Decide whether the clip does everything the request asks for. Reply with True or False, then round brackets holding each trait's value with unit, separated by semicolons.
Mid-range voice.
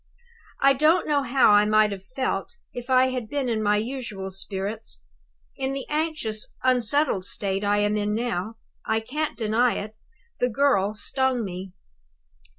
False (225 Hz)